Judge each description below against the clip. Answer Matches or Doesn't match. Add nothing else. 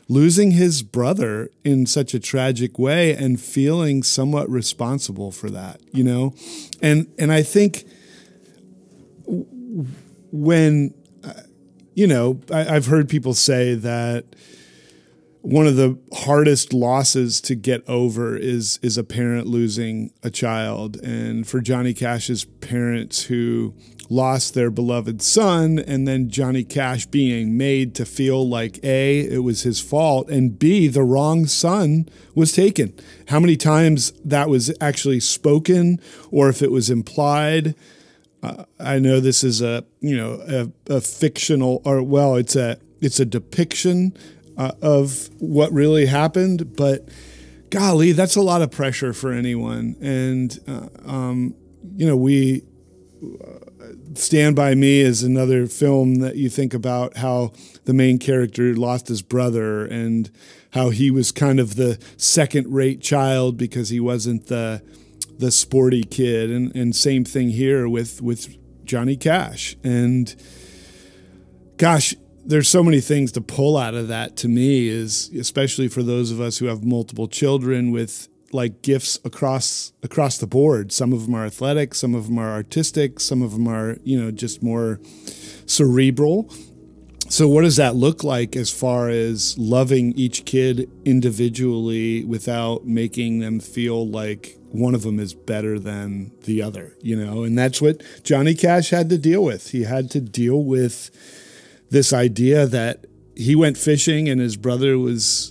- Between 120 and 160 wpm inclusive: Matches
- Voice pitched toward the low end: Matches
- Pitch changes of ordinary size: Matches